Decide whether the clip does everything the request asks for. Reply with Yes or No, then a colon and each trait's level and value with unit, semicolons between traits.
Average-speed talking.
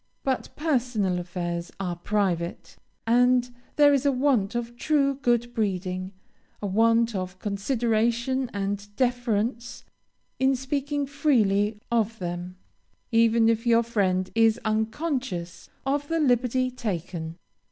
No: slow, 120 wpm